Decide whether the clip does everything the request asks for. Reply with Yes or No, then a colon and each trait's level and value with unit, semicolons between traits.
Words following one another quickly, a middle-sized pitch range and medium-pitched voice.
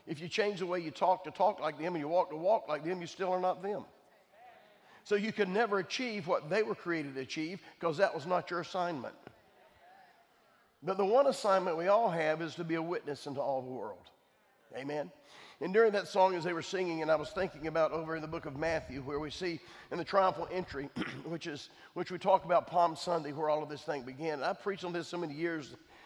Yes: fast, 240 wpm; average, 3.0 semitones; medium, 170 Hz